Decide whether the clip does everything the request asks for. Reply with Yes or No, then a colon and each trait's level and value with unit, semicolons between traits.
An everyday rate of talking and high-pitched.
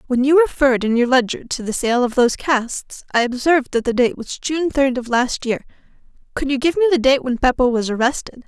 No: fast, 235 wpm; very high, 255 Hz